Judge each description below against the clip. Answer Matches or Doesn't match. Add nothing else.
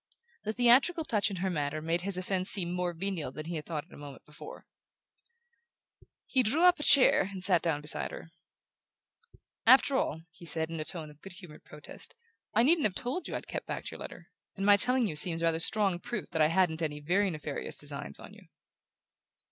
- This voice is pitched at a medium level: Matches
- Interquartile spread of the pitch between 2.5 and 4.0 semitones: Doesn't match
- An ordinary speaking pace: Doesn't match